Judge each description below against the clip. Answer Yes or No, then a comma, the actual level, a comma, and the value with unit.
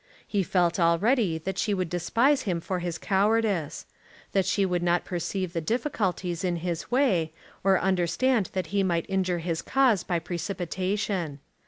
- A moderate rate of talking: Yes, average, 160 wpm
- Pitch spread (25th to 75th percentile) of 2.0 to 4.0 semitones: Yes, average, 2.9 semitones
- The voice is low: No, medium, 185 Hz